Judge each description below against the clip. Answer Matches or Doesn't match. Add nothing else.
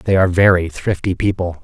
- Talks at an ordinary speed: Matches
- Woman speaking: Doesn't match